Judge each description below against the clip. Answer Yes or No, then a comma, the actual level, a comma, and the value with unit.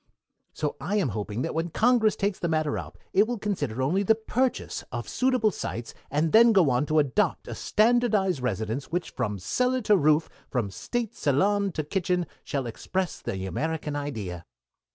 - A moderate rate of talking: Yes, average, 175 wpm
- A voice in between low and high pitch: Yes, medium, 165 Hz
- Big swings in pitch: Yes, wide, 7.9 semitones